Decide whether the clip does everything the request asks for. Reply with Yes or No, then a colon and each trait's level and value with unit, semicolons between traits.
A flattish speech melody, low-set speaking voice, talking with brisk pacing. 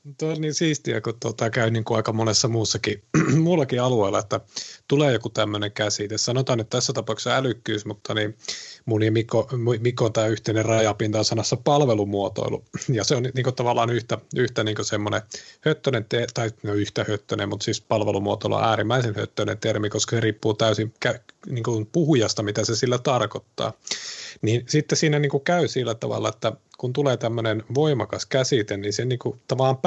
No: average, 3.1 semitones; low, 115 Hz; fast, 170 wpm